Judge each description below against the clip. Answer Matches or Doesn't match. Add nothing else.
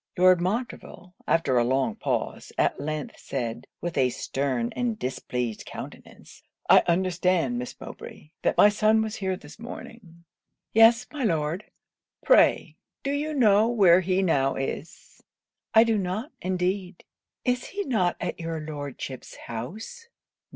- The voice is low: Doesn't match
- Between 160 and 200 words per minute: Doesn't match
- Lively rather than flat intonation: Matches